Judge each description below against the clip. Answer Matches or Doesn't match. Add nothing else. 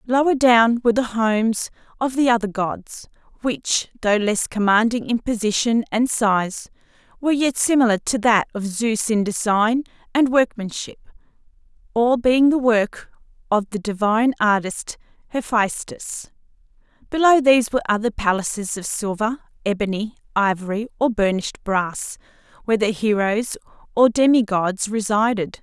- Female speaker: Matches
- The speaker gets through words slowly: Matches